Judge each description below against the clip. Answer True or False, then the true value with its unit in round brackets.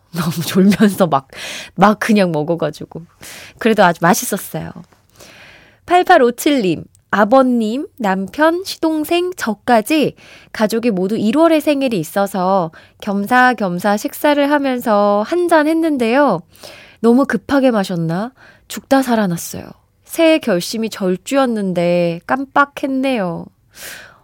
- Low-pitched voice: False (220 Hz)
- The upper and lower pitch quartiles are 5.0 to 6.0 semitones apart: False (6.8 semitones)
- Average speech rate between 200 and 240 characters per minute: True (235 characters per minute)